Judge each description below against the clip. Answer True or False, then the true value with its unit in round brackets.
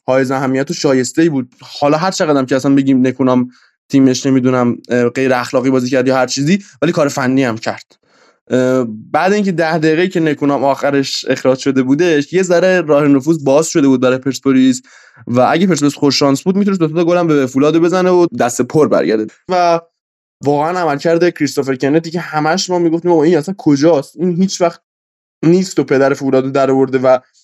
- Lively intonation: False (4.3 semitones)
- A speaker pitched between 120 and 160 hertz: True (140 Hz)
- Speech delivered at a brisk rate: True (190 wpm)